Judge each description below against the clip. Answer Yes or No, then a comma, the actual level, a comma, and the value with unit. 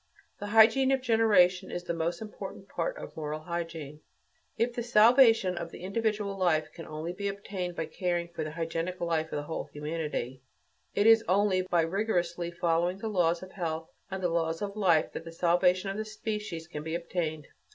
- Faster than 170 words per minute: Yes, average, 195 wpm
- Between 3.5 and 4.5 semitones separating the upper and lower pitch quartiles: Yes, average, 3.9 semitones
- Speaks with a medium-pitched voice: Yes, medium, 175 Hz